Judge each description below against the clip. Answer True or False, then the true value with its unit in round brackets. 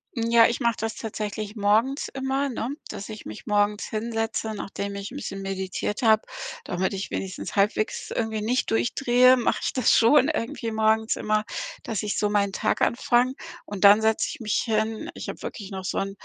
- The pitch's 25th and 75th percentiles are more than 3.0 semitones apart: False (2.4 semitones)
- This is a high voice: True (220 Hz)